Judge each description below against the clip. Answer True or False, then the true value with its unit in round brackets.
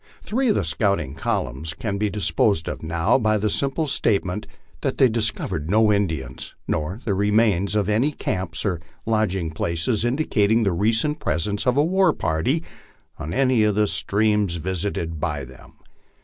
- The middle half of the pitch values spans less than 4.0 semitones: False (5.1 semitones)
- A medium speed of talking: True (170 wpm)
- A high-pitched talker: False (105 Hz)